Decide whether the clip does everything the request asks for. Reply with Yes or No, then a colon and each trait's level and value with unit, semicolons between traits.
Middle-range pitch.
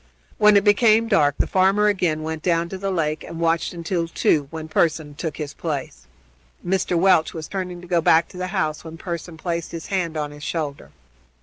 Yes: medium, 170 Hz